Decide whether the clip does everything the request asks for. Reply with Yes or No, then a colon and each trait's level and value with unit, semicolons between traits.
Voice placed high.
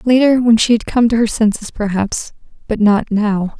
Yes: high, 220 Hz